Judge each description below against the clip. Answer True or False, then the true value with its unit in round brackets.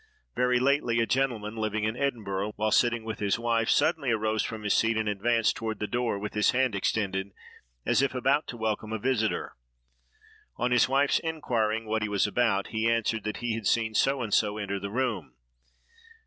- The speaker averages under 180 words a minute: False (195 wpm)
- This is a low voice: True (110 Hz)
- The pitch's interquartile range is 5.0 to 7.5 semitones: False (2.5 semitones)